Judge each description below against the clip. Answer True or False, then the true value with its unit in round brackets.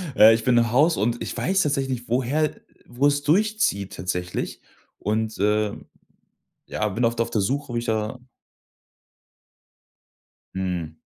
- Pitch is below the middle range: True (115 Hz)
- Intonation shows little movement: False (4.4 semitones)